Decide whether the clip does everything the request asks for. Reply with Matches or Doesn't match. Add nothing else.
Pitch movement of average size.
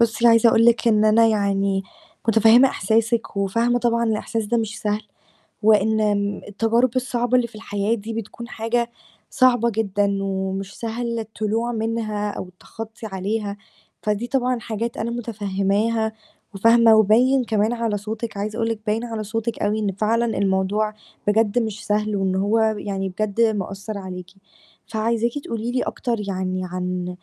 Doesn't match